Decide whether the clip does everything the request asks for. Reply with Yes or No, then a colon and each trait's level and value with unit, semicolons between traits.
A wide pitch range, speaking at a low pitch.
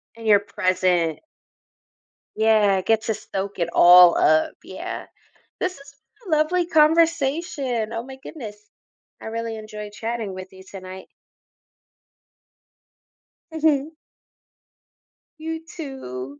No: wide, 7.7 semitones; high, 220 Hz